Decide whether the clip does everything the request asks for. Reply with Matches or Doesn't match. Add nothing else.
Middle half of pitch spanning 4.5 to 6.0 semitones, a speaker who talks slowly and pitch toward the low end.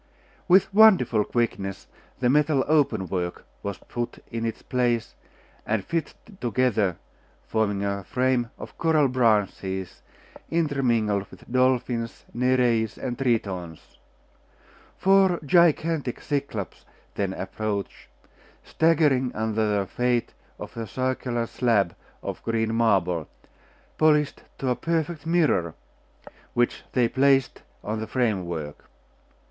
Matches